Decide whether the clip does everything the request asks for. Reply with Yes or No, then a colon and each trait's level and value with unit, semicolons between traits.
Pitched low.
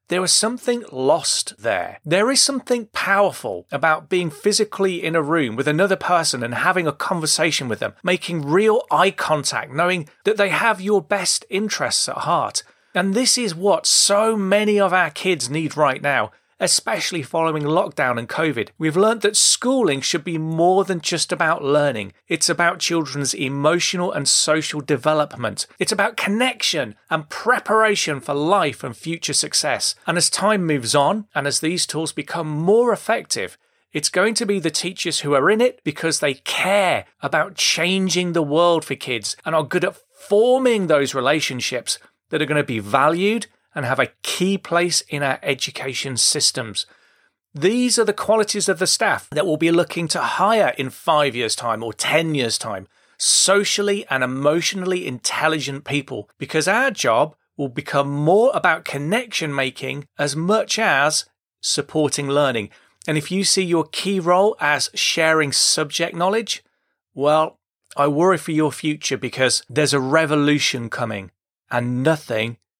No: medium, 160 Hz